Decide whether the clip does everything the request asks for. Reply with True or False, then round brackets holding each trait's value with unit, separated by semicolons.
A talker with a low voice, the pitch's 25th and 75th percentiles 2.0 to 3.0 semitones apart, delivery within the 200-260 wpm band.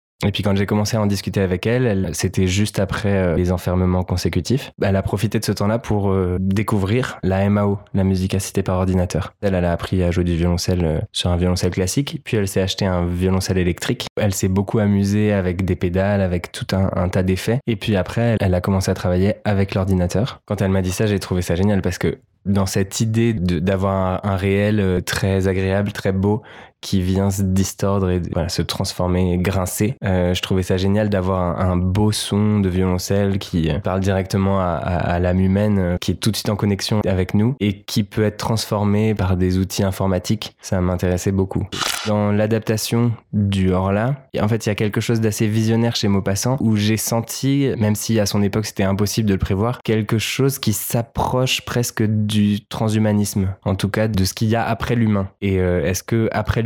True (100 Hz; 2.4 semitones; 215 wpm)